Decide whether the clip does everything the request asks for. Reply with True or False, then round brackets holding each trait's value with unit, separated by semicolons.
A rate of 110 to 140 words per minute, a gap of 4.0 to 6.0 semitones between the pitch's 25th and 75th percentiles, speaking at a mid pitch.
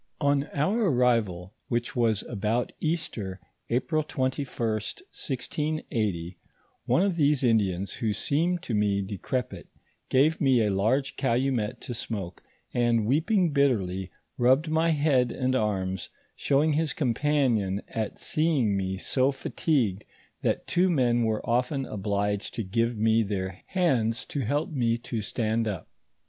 False (135 wpm; 5.3 semitones; 120 Hz)